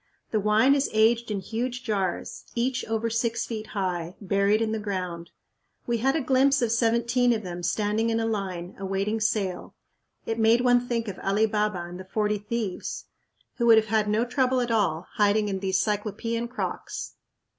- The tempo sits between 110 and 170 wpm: No, average, 185 wpm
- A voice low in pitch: No, high, 220 Hz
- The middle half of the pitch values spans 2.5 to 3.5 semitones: Yes, average, 2.9 semitones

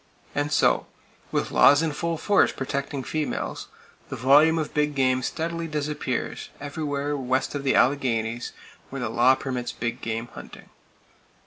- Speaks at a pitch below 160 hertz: Yes, medium, 140 Hz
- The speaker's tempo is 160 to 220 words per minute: No, average, 145 wpm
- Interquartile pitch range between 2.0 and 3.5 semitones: Yes, average, 2.8 semitones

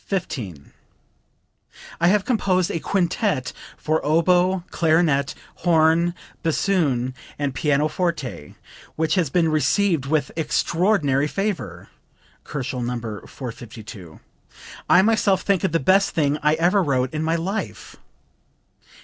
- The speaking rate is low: Yes, slow, 110 wpm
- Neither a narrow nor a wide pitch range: Yes, average, 4.6 semitones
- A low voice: No, medium, 160 Hz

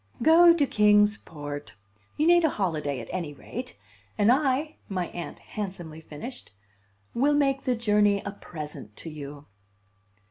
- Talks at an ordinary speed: Yes, average, 145 wpm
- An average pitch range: No, wide, 9.0 semitones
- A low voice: No, high, 205 Hz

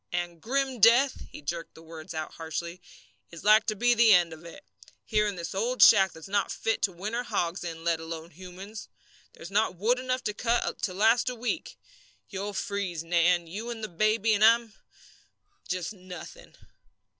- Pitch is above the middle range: Yes, high, 195 Hz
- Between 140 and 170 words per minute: No, average, 180 wpm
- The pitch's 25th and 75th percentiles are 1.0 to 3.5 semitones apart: No, average, 4.8 semitones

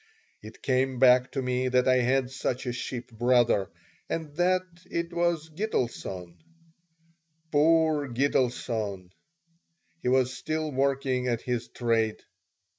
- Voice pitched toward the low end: Yes, low, 130 Hz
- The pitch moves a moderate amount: Yes, average, 3.2 semitones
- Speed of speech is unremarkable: No, slow, 120 wpm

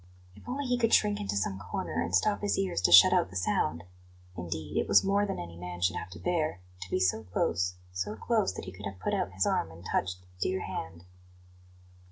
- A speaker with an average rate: No, fast, 235 wpm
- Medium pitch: No, very low, 95 Hz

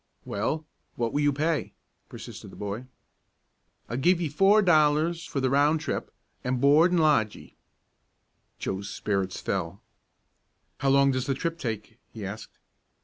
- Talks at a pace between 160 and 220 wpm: No, average, 150 wpm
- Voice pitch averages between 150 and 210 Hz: No, medium, 140 Hz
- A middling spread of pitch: No, wide, 5.7 semitones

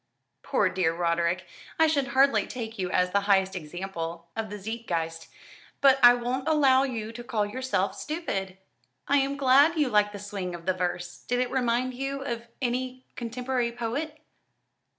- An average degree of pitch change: No, wide, 5.7 semitones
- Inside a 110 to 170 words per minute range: Yes, average, 165 wpm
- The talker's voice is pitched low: No, high, 235 Hz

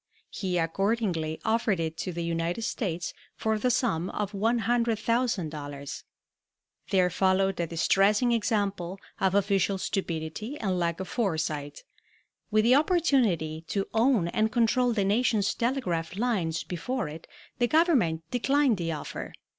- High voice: Yes, high, 195 Hz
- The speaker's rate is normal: No, slow, 130 wpm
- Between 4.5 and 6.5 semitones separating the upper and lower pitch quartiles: Yes, wide, 5.6 semitones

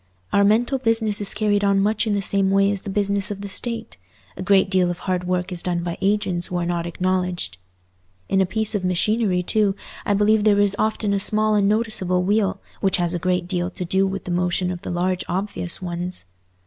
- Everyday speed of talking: No, fast, 220 wpm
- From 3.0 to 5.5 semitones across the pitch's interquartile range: No, narrow, 2.4 semitones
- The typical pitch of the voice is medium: No, high, 195 Hz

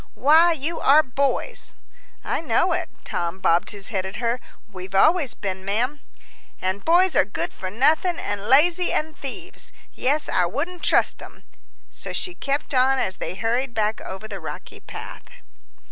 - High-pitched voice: Yes, very high, 260 Hz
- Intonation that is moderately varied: No, wide, 8.0 semitones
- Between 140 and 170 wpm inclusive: Yes, average, 165 wpm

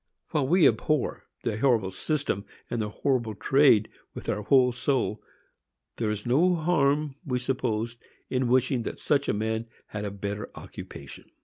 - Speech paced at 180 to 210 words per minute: No, average, 155 wpm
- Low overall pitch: Yes, low, 125 Hz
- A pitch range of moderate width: Yes, average, 4.5 semitones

